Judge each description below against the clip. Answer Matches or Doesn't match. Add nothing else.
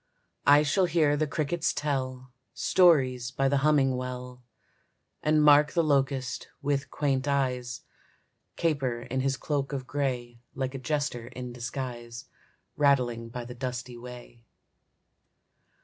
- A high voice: Doesn't match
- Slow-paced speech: Matches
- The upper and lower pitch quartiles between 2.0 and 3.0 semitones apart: Matches